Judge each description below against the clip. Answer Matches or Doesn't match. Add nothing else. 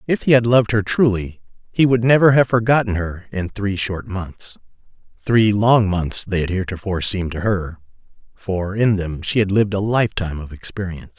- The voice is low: Matches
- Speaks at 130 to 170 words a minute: Doesn't match